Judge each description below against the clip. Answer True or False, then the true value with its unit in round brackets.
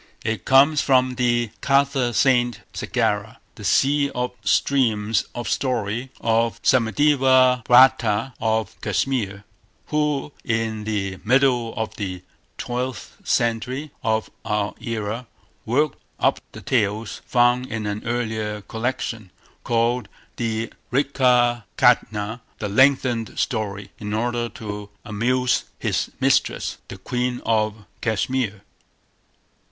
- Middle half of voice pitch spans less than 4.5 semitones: True (2.9 semitones)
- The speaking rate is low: True (110 wpm)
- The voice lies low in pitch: True (120 Hz)